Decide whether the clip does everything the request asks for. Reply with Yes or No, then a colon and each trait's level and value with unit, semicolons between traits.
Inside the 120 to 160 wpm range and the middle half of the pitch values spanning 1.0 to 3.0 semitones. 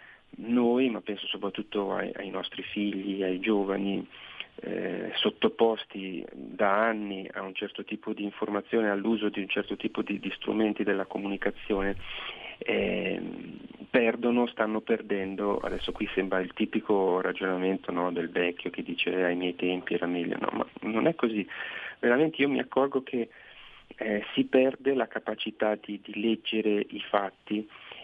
Yes: average, 150 wpm; narrow, 2.6 semitones